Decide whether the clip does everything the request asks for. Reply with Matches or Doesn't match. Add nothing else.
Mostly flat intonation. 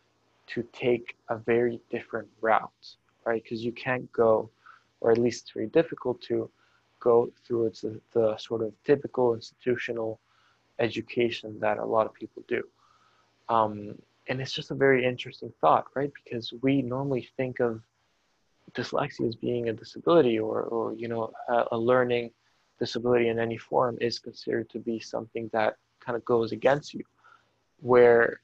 Matches